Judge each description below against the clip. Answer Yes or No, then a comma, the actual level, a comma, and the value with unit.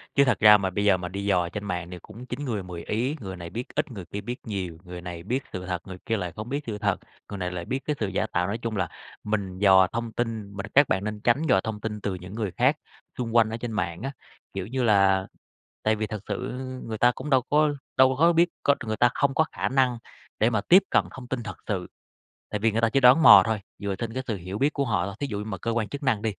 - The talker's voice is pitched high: No, low, 110 Hz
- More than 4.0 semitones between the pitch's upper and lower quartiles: Yes, average, 4.5 semitones